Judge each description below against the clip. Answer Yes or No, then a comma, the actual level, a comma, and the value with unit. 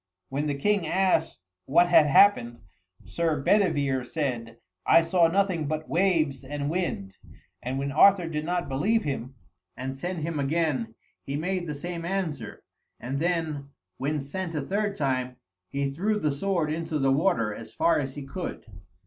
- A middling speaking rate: Yes, average, 165 wpm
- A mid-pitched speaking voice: Yes, medium, 155 Hz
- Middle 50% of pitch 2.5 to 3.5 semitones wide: No, average, 4.4 semitones